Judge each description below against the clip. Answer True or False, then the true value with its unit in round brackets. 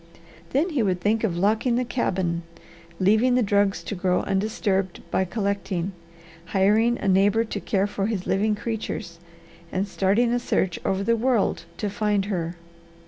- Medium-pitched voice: False (200 Hz)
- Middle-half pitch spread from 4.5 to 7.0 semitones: False (2.9 semitones)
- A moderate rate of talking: True (160 wpm)